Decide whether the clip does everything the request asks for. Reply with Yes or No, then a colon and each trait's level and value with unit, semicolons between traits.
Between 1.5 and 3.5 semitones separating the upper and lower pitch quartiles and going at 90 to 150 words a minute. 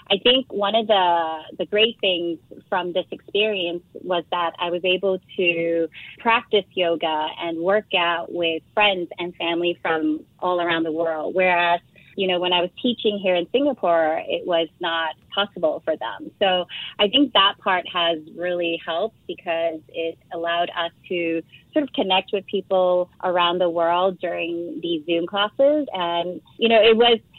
No: average, 3.1 semitones; average, 170 wpm